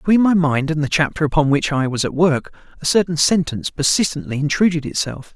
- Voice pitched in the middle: Yes, medium, 155 Hz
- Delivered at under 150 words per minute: No, average, 200 wpm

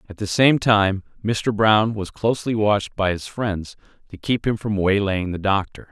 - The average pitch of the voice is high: No, low, 105 Hz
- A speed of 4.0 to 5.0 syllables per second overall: Yes, 4.6 syllables/s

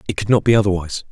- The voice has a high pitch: No, low, 100 Hz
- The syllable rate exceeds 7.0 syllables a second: Yes, 8.9 syllables/s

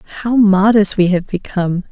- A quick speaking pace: No, average, 155 wpm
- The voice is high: Yes, high, 200 Hz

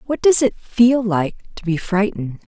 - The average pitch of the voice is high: Yes, high, 210 Hz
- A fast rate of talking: No, average, 190 wpm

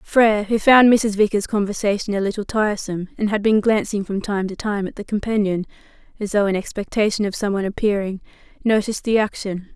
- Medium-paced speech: Yes, average, 185 wpm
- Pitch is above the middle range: Yes, high, 205 Hz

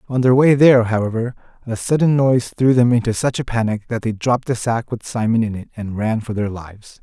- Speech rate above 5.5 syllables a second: Yes, 5.9 syllables/s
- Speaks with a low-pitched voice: Yes, low, 115 Hz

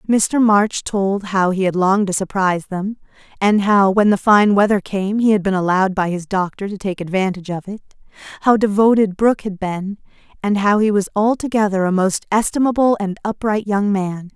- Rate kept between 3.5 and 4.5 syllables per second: No, 5.2 syllables/s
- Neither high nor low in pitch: No, high, 200 Hz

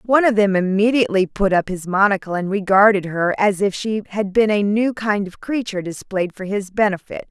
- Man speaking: No, female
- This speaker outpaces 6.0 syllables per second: No, 5.5 syllables/s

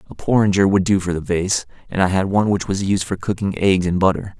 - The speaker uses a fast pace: Yes, fast, 260 wpm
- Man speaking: Yes, male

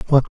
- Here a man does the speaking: Yes, male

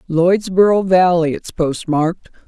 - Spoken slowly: Yes, slow, 95 wpm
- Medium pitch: Yes, medium, 175 Hz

